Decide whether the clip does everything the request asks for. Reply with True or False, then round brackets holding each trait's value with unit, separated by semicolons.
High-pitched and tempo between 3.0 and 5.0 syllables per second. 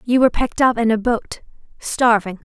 False (230 Hz; 5.5 syllables/s)